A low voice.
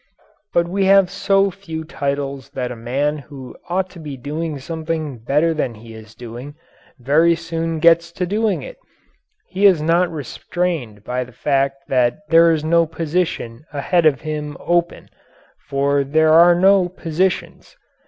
No: medium, 155 Hz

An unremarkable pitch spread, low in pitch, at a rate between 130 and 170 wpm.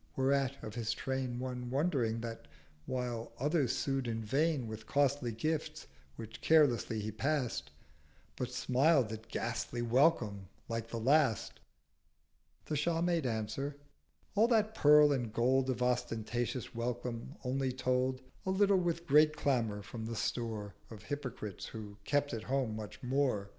Yes: average, 3.9 semitones; low, 125 Hz; average, 140 wpm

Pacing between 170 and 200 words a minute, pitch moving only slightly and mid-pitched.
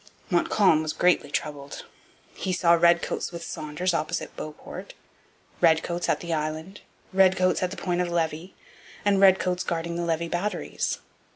No: average, 145 wpm; narrow, 2.3 semitones; medium, 170 Hz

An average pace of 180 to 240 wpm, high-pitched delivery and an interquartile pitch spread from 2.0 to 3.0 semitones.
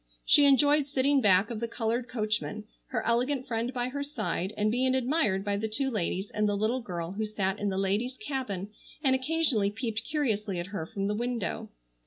No: average, 200 wpm; high, 225 Hz; average, 4.3 semitones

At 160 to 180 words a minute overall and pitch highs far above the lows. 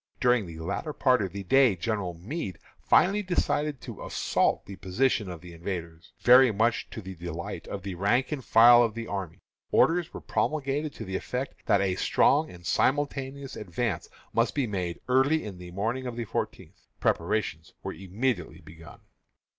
Yes: average, 175 wpm; wide, 6.6 semitones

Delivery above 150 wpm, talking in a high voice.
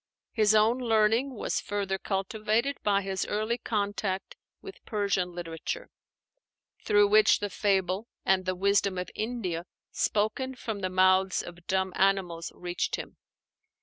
No: slow, 135 wpm; high, 200 Hz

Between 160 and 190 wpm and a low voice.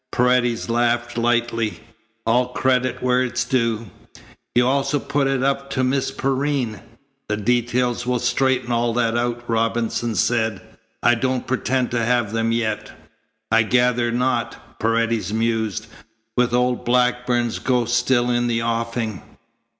No: average, 140 wpm; low, 120 Hz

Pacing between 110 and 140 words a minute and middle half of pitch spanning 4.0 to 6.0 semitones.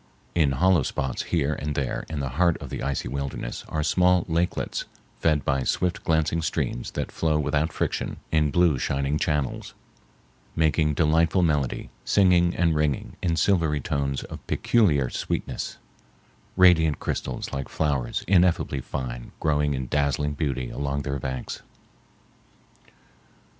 No: slow, 135 wpm; average, 3.2 semitones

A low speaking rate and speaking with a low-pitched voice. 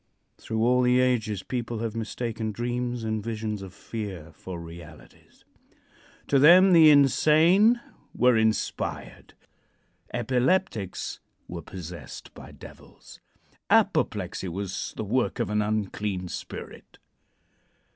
Yes: slow, 110 wpm; low, 110 Hz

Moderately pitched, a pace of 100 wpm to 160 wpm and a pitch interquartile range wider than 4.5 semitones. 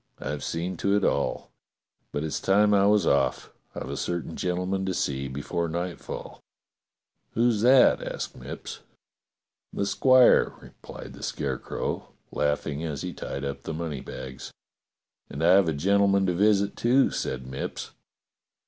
No: very low, 85 Hz; average, 155 wpm; wide, 5.6 semitones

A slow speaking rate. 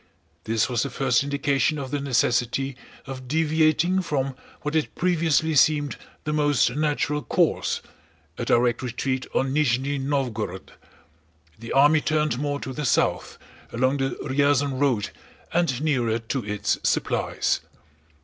Yes: slow, 130 wpm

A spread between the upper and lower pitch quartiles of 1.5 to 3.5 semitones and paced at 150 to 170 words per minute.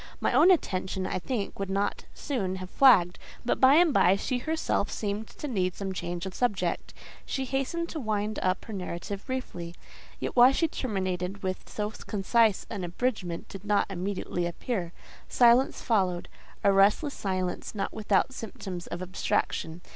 No: average, 4.9 semitones; average, 160 wpm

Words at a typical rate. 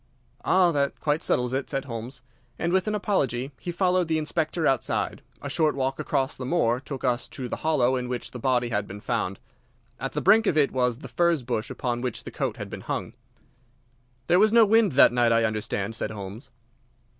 No: fast, 210 wpm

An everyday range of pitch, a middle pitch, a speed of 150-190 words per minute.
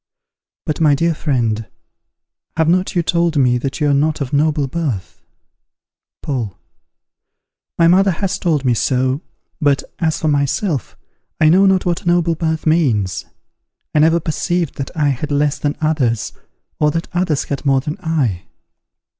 Yes: average, 3.4 semitones; medium, 150 Hz; average, 160 wpm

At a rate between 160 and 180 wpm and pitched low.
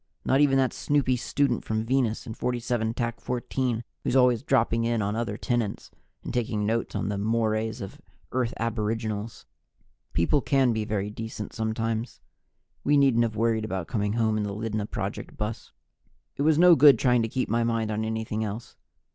Yes: average, 175 wpm; low, 115 Hz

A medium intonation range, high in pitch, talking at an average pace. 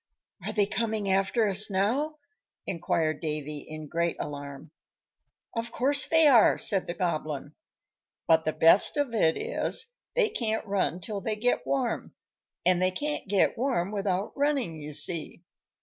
No: wide, 6.4 semitones; high, 195 Hz; average, 150 wpm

